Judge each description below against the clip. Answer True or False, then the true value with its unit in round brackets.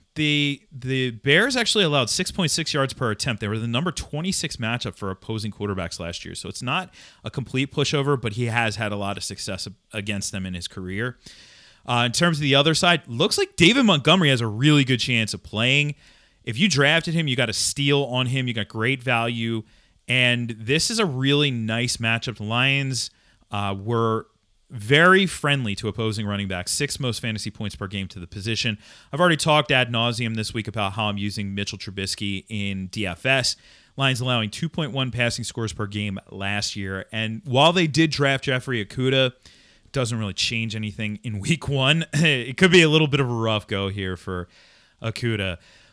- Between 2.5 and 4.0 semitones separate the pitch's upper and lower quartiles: False (5.1 semitones)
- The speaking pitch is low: True (120 Hz)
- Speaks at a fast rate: False (195 wpm)